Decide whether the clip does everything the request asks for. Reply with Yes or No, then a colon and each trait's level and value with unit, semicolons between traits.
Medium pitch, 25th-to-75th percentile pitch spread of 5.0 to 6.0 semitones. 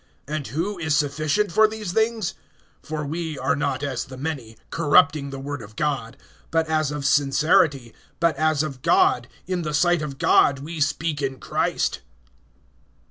No: medium, 150 Hz; average, 2.9 semitones